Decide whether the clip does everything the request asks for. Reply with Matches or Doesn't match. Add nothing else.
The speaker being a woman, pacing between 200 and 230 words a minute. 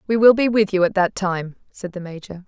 Doesn't match